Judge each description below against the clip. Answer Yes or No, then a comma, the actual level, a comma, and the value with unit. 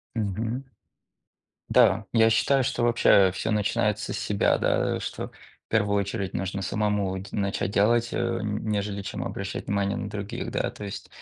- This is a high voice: No, low, 105 Hz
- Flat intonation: Yes, narrow, 1.9 semitones